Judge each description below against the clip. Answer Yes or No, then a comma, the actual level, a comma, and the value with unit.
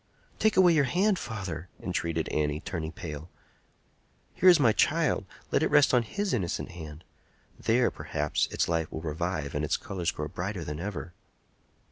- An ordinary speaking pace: Yes, average, 165 wpm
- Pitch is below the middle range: Yes, very low, 90 Hz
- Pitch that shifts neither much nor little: No, wide, 8.0 semitones